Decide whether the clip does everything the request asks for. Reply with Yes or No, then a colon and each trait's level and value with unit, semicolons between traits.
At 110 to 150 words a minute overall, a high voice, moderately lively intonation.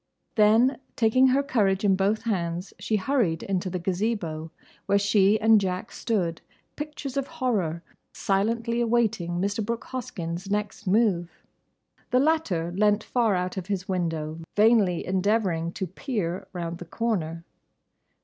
Yes: average, 140 wpm; high, 200 Hz; average, 4.4 semitones